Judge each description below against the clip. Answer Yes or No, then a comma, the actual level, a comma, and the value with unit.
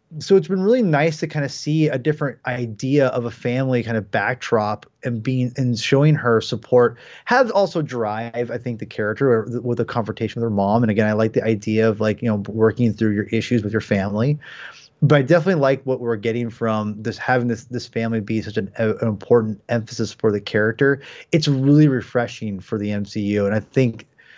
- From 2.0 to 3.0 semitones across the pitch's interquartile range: No, average, 3.8 semitones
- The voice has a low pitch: Yes, low, 120 Hz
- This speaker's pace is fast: Yes, fast, 215 wpm